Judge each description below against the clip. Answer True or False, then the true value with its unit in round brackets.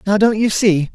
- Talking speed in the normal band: False (255 wpm)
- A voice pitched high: True (200 Hz)